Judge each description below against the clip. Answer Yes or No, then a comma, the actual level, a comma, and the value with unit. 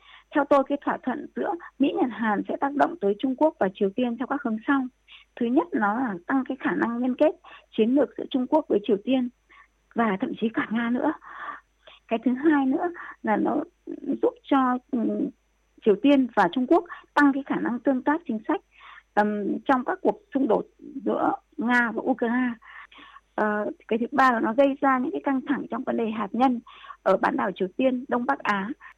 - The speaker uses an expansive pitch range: No, average, 4.1 semitones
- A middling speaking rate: Yes, average, 205 wpm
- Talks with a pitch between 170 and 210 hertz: No, very high, 275 Hz